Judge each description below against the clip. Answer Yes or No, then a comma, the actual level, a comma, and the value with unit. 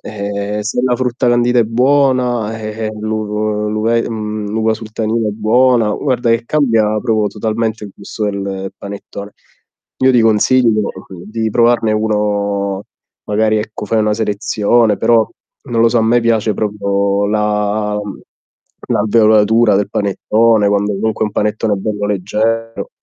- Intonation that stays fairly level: Yes, narrow, 1.7 semitones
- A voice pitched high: No, low, 110 Hz